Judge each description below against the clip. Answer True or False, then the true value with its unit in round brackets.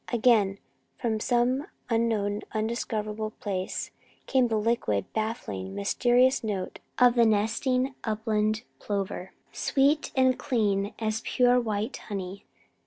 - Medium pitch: False (220 Hz)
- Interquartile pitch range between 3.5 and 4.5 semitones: False (3.1 semitones)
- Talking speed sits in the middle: False (110 wpm)